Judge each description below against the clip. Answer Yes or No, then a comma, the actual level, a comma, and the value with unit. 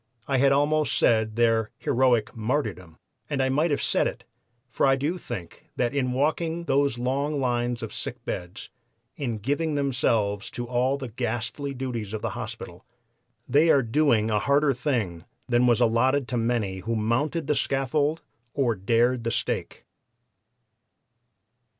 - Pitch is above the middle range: No, low, 125 Hz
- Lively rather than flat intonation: No, average, 3.9 semitones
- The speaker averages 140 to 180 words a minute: Yes, average, 155 wpm